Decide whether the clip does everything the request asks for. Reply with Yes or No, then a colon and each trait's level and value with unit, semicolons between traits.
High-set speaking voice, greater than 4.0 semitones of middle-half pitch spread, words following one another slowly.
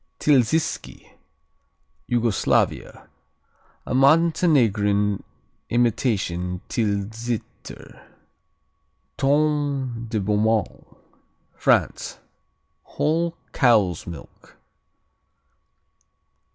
No: low, 115 Hz; wide, 5.5 semitones; slow, 45 wpm